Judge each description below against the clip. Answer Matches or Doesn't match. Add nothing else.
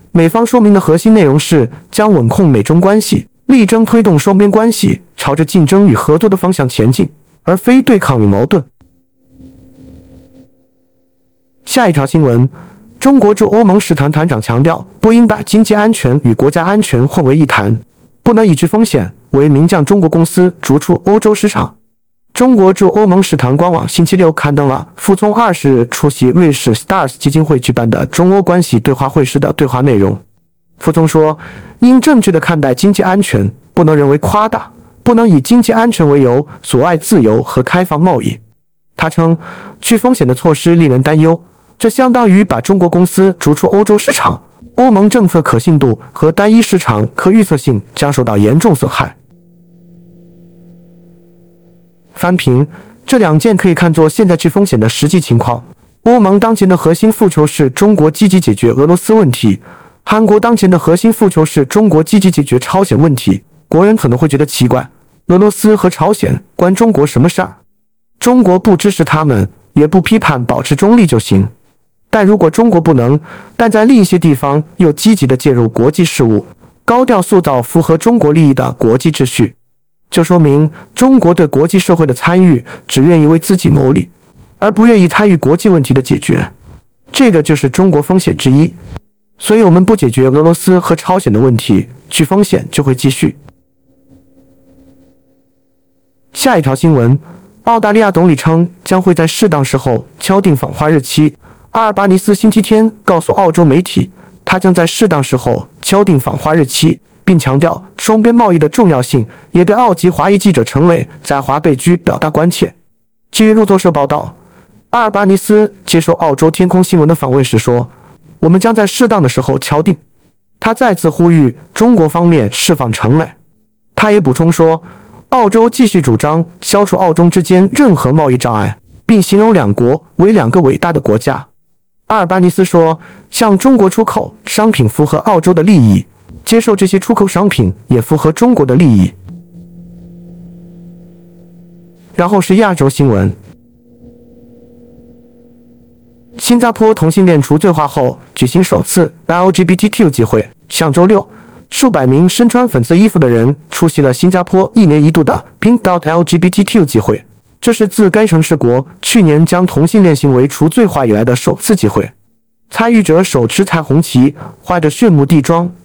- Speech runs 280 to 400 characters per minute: Doesn't match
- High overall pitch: Doesn't match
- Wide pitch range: Matches